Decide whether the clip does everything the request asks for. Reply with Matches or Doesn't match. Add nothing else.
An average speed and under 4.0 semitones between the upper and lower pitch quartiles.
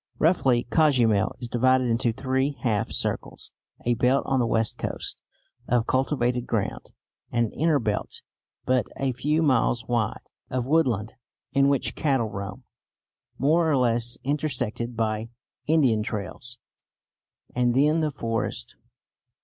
Doesn't match